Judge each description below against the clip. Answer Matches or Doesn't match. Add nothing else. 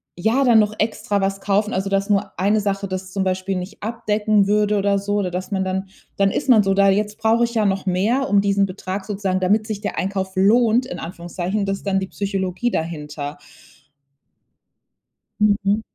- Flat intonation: Matches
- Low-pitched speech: Doesn't match